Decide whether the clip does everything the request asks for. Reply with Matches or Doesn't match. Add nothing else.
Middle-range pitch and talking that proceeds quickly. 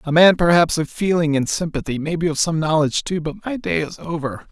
Matches